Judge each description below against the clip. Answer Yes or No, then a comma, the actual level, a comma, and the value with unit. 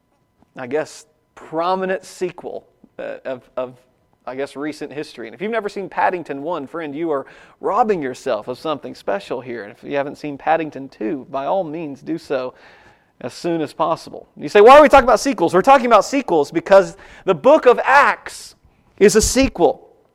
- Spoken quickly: No, average, 185 wpm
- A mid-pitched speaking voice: Yes, medium, 160 Hz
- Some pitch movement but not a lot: No, wide, 5.7 semitones